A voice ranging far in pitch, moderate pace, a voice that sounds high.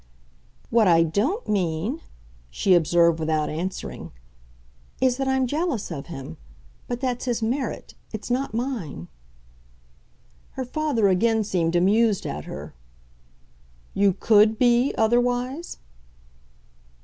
No: wide, 6.3 semitones; slow, 115 wpm; high, 220 Hz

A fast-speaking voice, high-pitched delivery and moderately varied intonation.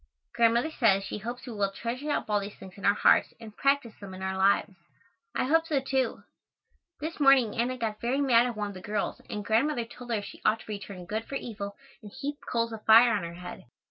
Yes: fast, 235 wpm; high, 225 Hz; average, 3.9 semitones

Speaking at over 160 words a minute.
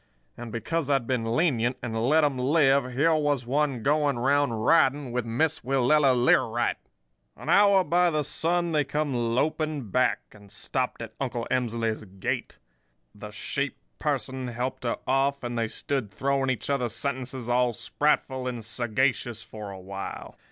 No: average, 155 wpm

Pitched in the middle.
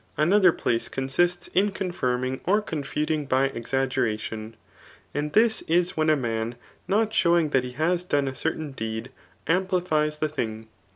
Yes: medium, 150 Hz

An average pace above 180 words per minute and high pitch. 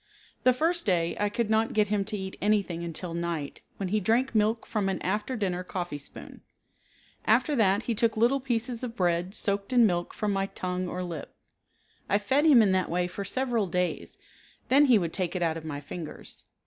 Yes: fast, 205 wpm; high, 200 Hz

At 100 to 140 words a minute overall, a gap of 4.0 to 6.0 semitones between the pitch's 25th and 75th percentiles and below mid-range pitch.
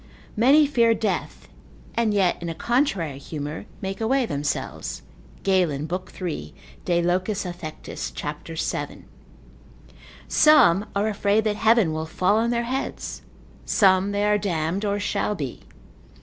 No: slow, 135 wpm; average, 4.7 semitones; high, 195 Hz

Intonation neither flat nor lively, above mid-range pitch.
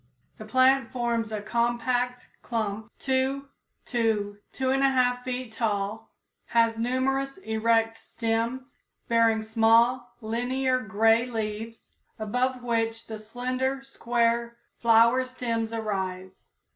No: narrow, 2.2 semitones; high, 235 Hz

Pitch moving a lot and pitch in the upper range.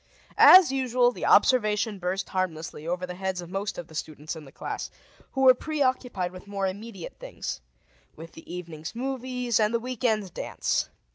Yes: wide, 5.8 semitones; high, 200 Hz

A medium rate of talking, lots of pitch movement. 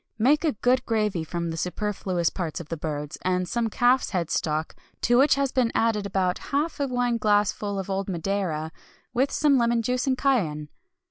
Yes: average, 190 wpm; wide, 6.1 semitones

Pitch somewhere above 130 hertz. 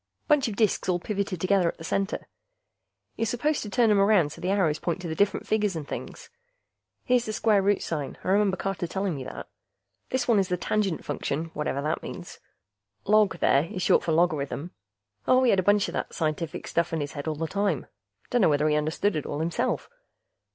Yes: medium, 185 Hz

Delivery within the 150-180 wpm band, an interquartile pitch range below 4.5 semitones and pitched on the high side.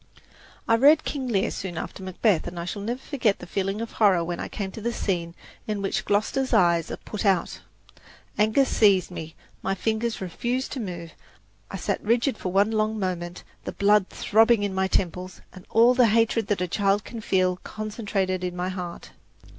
No: average, 195 wpm; average, 3.5 semitones; high, 200 Hz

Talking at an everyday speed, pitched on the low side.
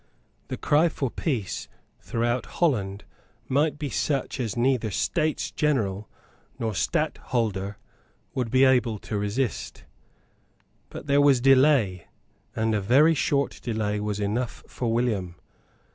No: slow, 125 wpm; low, 120 Hz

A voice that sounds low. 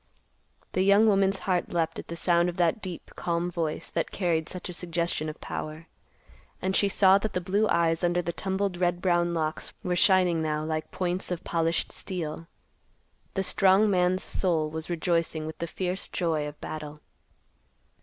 No: medium, 175 Hz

